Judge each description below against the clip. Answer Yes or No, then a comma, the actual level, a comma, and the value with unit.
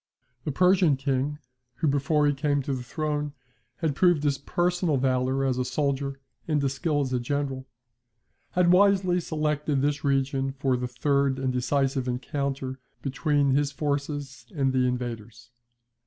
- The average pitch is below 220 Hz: Yes, medium, 140 Hz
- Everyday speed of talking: Yes, average, 155 wpm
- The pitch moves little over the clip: Yes, narrow, 2.1 semitones